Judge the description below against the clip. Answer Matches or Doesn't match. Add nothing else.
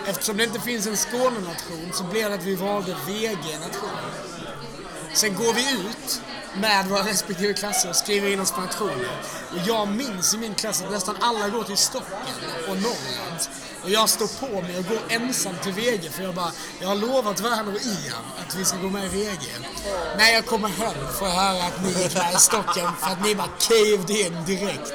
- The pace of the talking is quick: Matches